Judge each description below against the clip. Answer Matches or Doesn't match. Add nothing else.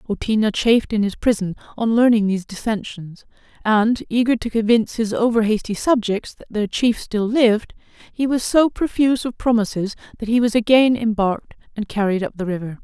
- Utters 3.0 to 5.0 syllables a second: Doesn't match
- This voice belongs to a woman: Matches